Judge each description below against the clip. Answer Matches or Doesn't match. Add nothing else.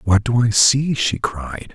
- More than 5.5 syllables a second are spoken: Doesn't match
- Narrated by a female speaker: Doesn't match